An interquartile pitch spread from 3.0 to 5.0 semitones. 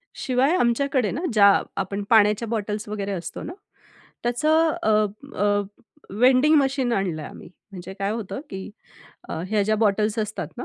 Yes: average, 3.8 semitones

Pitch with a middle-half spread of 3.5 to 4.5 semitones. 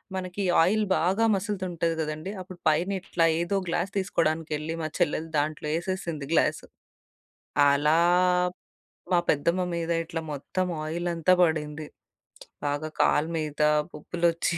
No: average, 2.8 semitones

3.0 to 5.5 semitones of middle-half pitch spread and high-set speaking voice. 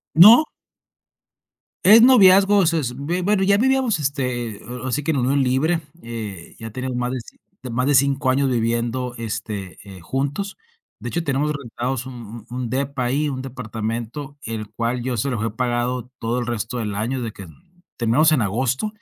No: average, 3.8 semitones; low, 125 Hz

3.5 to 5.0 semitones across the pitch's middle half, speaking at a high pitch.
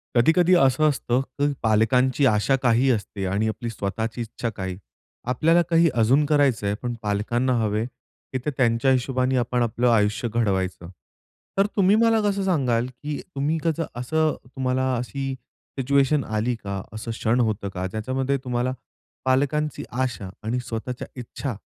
No: average, 3.8 semitones; low, 125 Hz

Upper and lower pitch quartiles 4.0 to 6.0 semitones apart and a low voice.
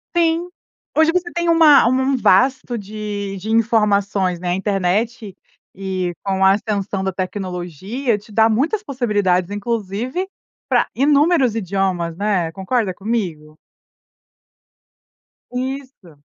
No: average, 5.2 semitones; high, 210 Hz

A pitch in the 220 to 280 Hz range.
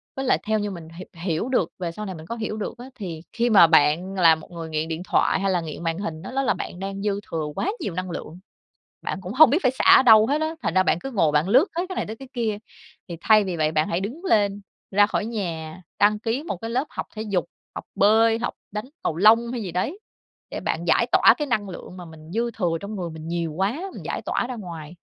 No: high, 195 Hz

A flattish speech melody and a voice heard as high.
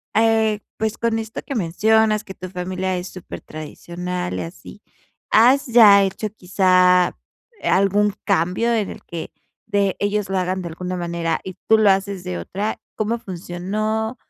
No: average, 3.3 semitones; high, 195 Hz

